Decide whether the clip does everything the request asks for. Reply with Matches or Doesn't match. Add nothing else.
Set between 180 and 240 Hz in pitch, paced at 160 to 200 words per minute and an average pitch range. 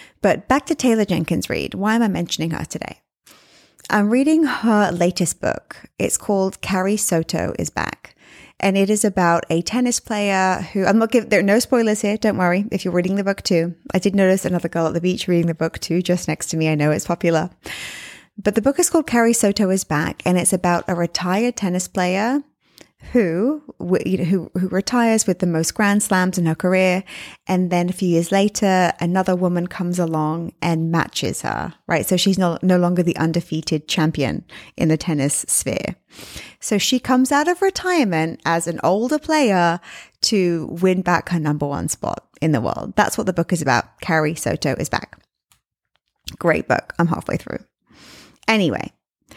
Matches